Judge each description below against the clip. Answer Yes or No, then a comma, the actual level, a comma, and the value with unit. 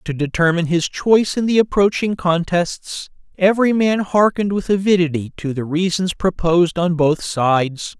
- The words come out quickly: No, average, 150 wpm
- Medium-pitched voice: Yes, medium, 180 Hz